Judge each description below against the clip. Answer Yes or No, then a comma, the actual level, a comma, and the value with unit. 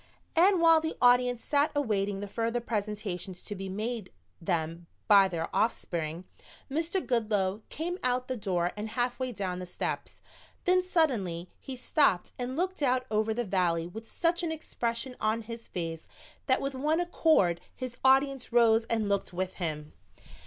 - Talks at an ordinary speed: Yes, average, 160 wpm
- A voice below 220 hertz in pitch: No, high, 230 Hz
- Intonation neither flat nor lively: No, wide, 6.0 semitones